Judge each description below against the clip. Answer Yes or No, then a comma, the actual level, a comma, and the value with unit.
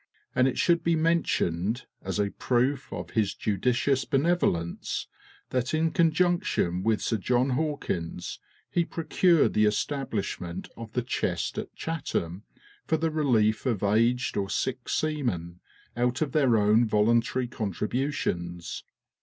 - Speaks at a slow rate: Yes, slow, 130 wpm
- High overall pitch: No, low, 120 Hz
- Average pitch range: No, wide, 6.1 semitones